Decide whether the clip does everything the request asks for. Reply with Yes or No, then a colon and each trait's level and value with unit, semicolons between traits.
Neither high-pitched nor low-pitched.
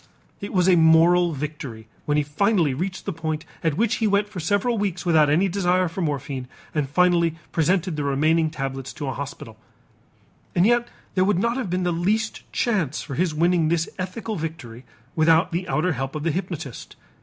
Yes: medium, 170 Hz